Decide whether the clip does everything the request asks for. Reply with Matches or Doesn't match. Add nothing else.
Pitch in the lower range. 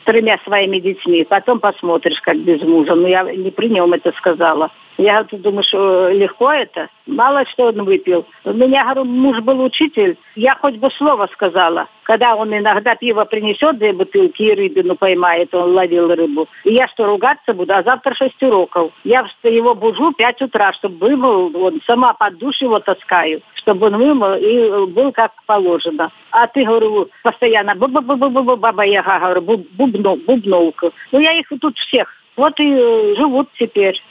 Doesn't match